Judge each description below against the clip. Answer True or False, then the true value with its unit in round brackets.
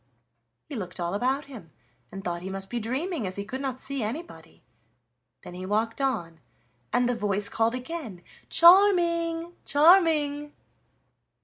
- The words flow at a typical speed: True (145 wpm)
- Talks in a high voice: True (250 Hz)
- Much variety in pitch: True (8.0 semitones)